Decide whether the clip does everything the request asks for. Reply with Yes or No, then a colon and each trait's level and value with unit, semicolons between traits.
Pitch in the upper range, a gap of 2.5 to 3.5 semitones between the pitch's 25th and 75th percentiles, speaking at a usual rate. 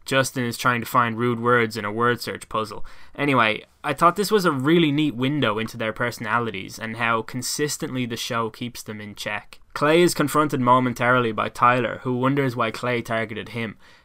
No: low, 120 Hz; average, 3.1 semitones; average, 190 wpm